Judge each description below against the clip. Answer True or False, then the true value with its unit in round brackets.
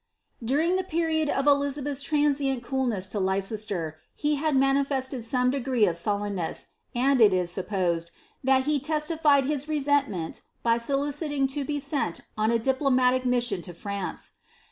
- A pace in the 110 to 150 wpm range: True (145 wpm)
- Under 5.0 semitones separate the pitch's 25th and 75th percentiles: False (5.4 semitones)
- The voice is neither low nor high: False (265 Hz)